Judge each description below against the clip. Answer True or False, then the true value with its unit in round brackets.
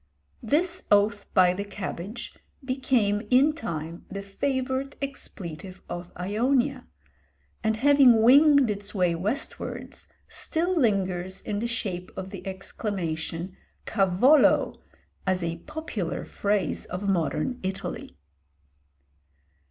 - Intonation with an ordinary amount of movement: False (6.0 semitones)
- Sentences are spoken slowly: True (105 wpm)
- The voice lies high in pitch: True (205 Hz)